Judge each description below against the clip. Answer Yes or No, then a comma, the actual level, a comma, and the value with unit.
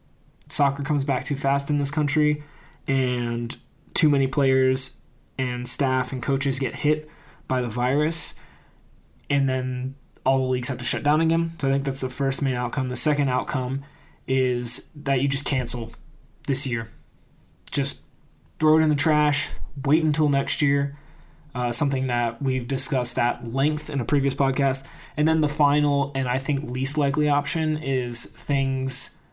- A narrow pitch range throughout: Yes, narrow, 2.2 semitones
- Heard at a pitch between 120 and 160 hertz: Yes, low, 135 Hz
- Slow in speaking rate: No, average, 170 wpm